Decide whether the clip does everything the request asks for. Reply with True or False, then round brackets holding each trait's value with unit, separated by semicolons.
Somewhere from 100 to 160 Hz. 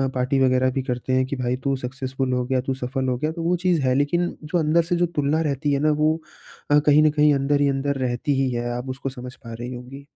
True (135 Hz)